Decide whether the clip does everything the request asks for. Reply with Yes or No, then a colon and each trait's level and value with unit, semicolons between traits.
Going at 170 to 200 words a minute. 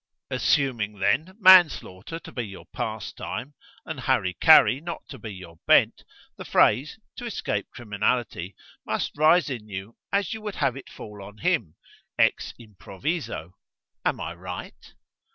No: average, 145 wpm